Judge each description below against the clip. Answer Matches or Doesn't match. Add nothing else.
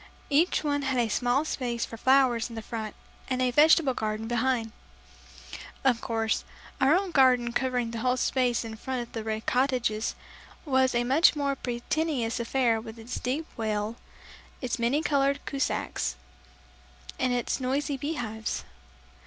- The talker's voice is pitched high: Matches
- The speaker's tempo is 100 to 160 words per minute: Matches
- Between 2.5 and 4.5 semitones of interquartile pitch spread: Matches